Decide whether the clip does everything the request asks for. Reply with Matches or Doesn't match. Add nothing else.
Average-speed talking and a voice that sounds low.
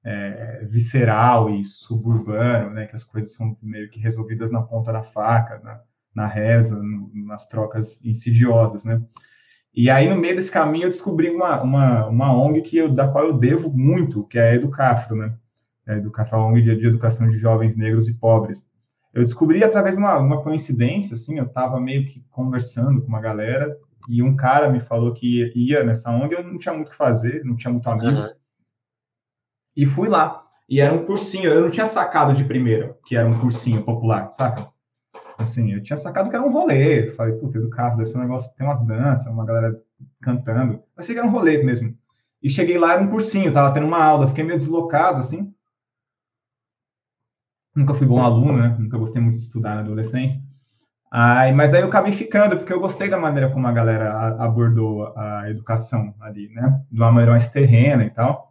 Doesn't match